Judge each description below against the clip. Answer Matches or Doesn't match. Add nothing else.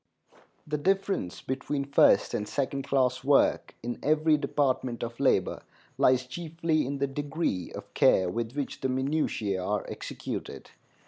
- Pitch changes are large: Doesn't match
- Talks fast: Doesn't match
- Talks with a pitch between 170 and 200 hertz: Doesn't match